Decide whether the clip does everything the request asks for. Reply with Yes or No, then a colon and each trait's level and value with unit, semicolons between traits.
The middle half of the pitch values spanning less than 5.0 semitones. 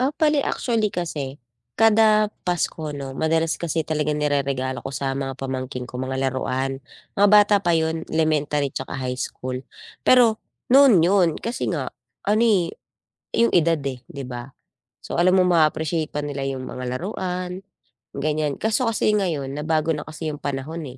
No: wide, 5.4 semitones